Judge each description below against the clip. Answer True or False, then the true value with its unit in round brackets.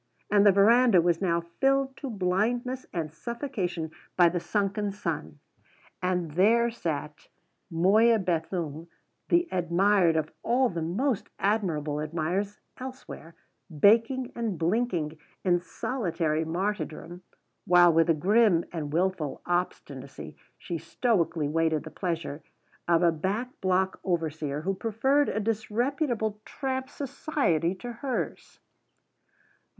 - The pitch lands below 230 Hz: True (185 Hz)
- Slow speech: True (120 wpm)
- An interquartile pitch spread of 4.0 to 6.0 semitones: True (5.6 semitones)